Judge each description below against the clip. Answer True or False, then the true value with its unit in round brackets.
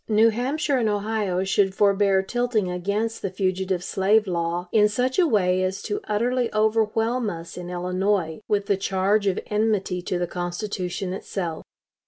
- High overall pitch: True (200 Hz)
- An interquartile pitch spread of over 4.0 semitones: False (3.0 semitones)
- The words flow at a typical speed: True (155 wpm)